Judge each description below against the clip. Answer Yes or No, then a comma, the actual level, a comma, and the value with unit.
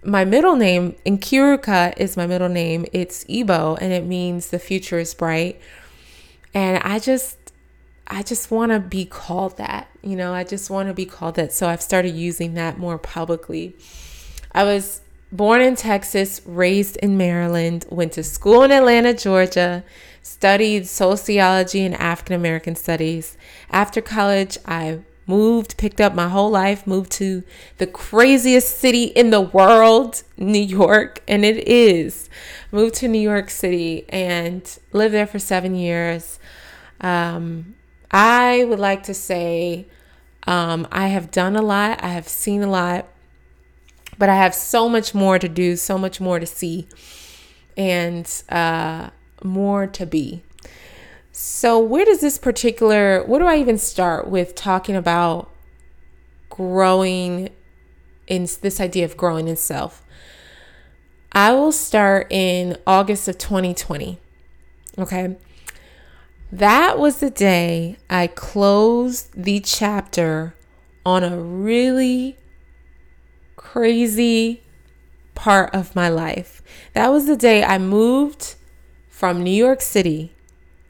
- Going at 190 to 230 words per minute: No, average, 140 wpm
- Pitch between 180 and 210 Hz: Yes, medium, 185 Hz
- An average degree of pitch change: Yes, average, 3.6 semitones